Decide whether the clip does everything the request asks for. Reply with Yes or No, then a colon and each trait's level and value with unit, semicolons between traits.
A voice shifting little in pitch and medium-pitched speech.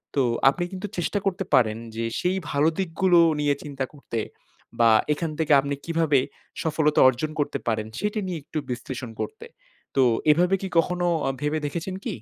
No: average, 4.4 semitones; medium, 155 Hz